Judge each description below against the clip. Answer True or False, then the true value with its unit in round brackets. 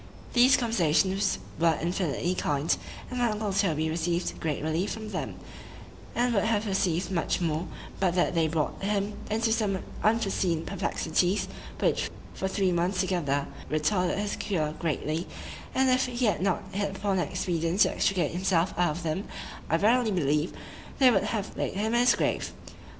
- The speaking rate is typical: True (165 wpm)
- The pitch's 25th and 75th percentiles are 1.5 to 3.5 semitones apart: False (4.0 semitones)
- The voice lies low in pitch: False (190 Hz)